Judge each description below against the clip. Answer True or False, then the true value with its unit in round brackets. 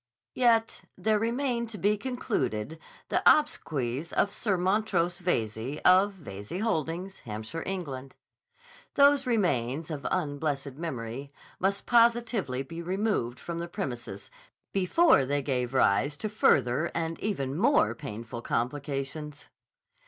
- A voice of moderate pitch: True (165 Hz)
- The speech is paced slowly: True (120 wpm)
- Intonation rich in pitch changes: True (7.7 semitones)